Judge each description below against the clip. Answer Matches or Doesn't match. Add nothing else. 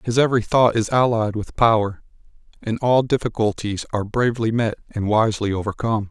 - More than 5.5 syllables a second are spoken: Matches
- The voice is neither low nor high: Doesn't match